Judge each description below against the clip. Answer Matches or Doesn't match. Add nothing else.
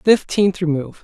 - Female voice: Doesn't match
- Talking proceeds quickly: Doesn't match